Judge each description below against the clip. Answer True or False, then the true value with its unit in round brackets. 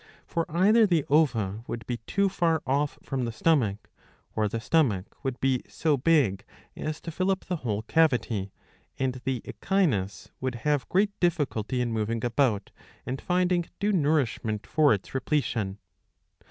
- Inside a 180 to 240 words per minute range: False (155 wpm)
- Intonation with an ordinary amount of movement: False (6.4 semitones)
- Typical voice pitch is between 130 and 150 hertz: True (135 Hz)